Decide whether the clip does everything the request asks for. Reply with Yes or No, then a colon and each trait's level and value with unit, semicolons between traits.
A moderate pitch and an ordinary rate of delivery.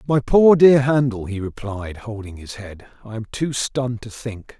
No: low, 120 Hz; average, 195 wpm